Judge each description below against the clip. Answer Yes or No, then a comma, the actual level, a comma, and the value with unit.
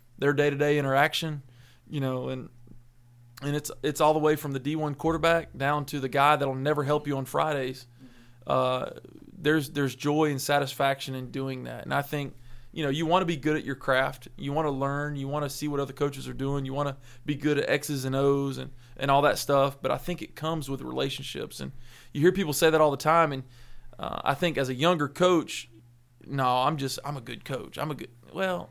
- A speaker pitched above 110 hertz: Yes, medium, 140 Hz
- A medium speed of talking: No, fast, 230 wpm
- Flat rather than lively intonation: Yes, narrow, 2.3 semitones